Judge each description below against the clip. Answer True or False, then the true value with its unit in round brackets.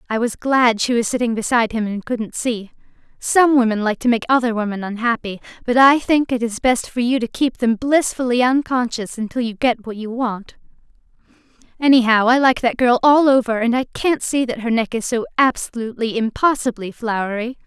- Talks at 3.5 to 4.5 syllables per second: False (5.4 syllables/s)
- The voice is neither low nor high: False (240 Hz)